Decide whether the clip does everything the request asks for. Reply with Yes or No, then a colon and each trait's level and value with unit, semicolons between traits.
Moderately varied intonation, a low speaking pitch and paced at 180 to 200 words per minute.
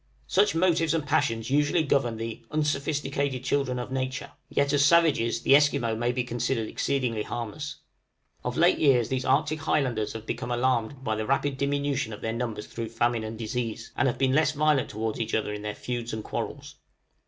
Yes: average, 3.8 semitones; low, 130 Hz; average, 190 wpm